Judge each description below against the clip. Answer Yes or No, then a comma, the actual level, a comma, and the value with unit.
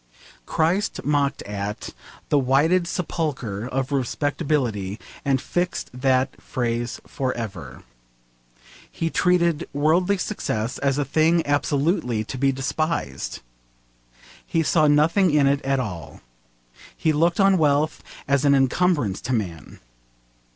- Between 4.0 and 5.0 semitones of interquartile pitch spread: Yes, average, 4.5 semitones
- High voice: No, medium, 140 Hz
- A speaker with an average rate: No, slow, 125 wpm